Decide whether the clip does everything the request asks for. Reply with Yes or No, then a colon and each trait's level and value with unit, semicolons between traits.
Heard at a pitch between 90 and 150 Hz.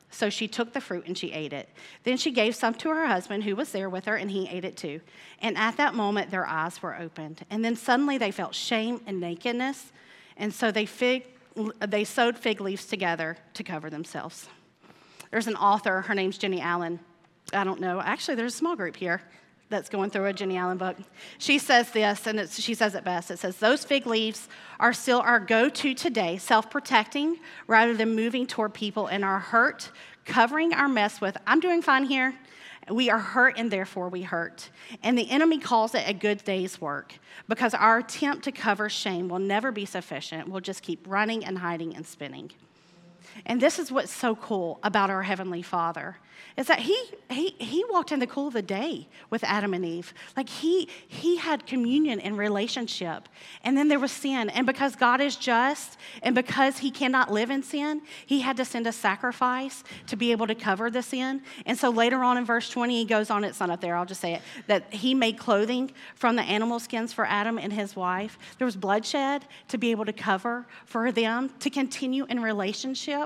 No: high, 225 Hz